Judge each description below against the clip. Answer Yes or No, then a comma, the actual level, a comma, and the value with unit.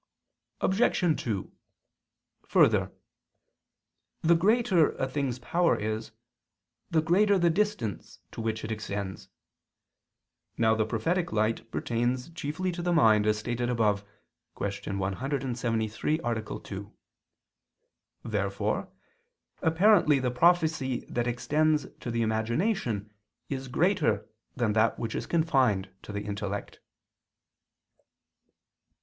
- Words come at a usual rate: No, slow, 110 wpm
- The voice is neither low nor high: No, low, 120 Hz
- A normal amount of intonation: No, wide, 7.0 semitones